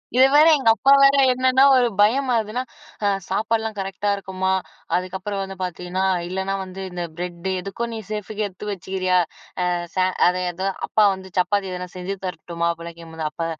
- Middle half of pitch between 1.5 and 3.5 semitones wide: Yes, average, 2.9 semitones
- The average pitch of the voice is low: No, high, 190 Hz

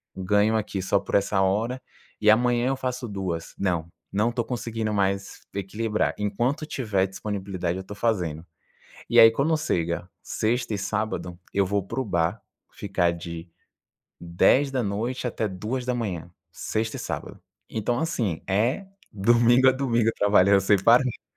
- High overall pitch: No, low, 105 Hz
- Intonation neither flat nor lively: Yes, average, 3.8 semitones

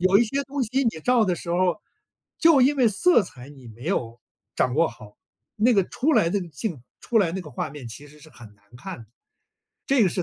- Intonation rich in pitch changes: Yes, wide, 8.8 semitones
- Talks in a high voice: No, medium, 180 Hz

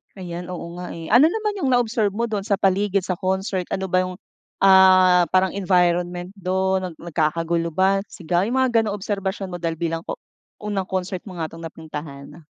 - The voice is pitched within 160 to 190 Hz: Yes, medium, 185 Hz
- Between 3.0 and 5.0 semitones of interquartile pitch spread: No, narrow, 2.4 semitones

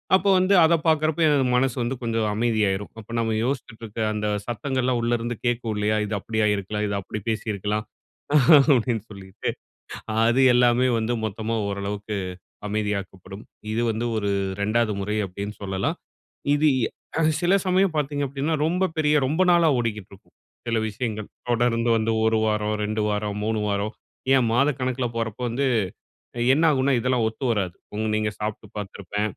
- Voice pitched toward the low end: Yes, low, 115 Hz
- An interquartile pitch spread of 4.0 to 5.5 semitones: No, average, 3.4 semitones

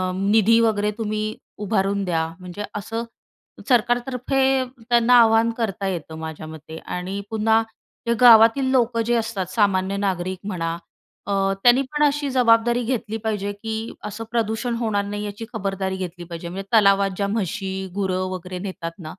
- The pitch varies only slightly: No, average, 3.3 semitones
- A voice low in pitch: No, high, 210 Hz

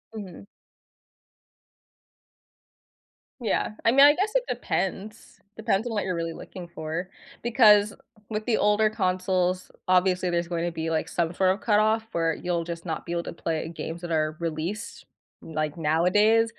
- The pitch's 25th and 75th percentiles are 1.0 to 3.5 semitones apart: No, average, 4.1 semitones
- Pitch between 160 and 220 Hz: Yes, medium, 185 Hz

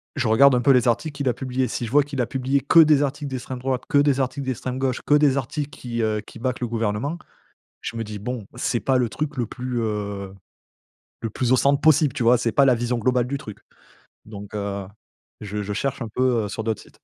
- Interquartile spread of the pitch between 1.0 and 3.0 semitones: No, average, 3.4 semitones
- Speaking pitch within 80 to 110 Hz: No, low, 125 Hz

